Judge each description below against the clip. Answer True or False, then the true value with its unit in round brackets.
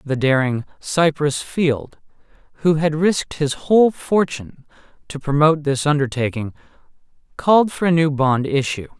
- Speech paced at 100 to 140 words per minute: True (135 wpm)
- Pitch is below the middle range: False (150 Hz)